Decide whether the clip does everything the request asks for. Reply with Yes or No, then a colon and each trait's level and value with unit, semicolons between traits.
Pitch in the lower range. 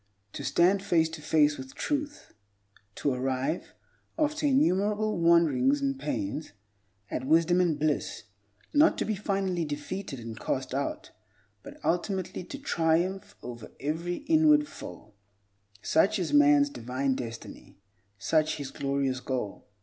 No: medium, 155 Hz